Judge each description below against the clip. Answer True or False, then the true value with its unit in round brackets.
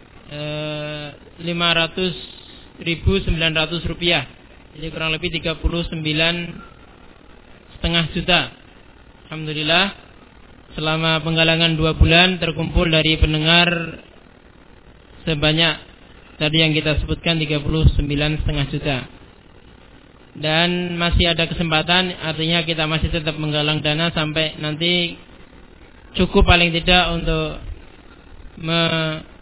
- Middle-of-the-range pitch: True (160 Hz)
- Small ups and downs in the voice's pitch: True (2.0 semitones)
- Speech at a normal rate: False (85 wpm)